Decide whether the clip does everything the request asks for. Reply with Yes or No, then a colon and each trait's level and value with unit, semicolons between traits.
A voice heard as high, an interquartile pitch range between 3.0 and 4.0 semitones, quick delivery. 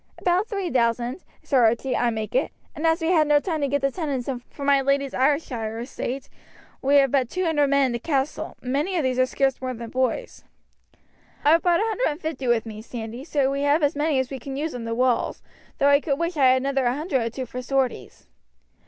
Yes: very high, 275 Hz; average, 3.4 semitones; fast, 240 wpm